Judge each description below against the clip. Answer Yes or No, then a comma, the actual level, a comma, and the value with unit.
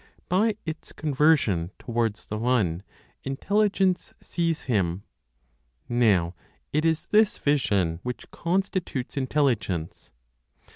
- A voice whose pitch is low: Yes, low, 130 Hz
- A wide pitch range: Yes, wide, 8.2 semitones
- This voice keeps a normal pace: No, slow, 95 wpm